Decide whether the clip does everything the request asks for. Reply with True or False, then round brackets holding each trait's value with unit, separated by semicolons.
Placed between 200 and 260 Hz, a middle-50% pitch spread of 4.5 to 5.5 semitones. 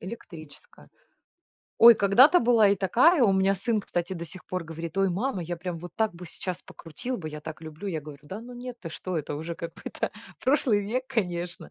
False (185 Hz; 5.2 semitones)